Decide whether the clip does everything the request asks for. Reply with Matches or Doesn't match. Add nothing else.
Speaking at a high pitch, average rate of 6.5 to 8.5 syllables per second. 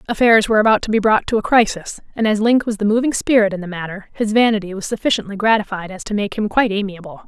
Matches